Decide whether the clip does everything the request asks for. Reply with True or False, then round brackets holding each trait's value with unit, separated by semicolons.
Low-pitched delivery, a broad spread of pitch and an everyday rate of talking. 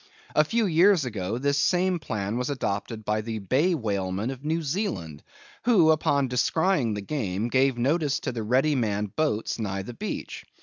True (125 Hz; 6.6 semitones; 175 wpm)